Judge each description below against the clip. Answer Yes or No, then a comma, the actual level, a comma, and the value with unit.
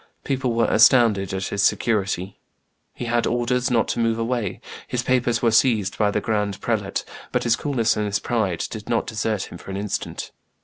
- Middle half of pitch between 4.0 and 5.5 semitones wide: No, average, 2.7 semitones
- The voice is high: No, low, 115 Hz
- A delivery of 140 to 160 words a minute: No, average, 190 wpm